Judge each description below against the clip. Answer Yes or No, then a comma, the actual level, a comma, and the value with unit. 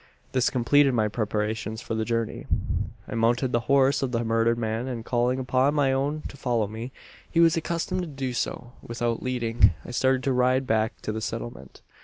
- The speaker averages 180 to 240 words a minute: Yes, average, 195 wpm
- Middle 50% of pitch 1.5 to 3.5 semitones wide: Yes, average, 2.8 semitones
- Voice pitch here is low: Yes, low, 120 Hz